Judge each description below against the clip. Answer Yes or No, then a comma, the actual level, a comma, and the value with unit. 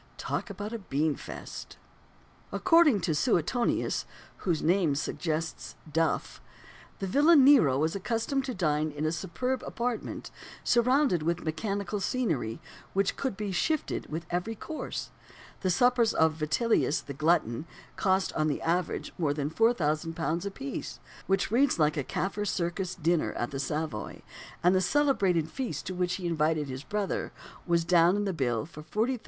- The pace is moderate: Yes, average, 155 wpm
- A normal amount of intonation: No, wide, 6.0 semitones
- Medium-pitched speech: Yes, medium, 180 Hz